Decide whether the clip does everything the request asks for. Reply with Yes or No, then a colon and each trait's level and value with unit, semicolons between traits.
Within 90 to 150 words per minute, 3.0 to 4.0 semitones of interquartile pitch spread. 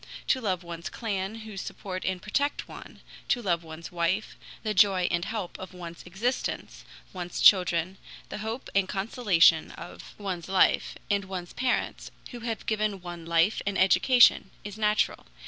No: average, 160 wpm; average, 3.4 semitones